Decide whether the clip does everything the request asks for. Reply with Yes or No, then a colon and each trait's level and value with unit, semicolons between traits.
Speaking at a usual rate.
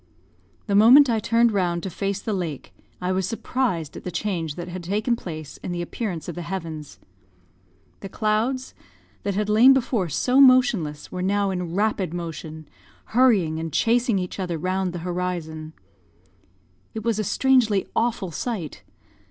Yes: average, 160 wpm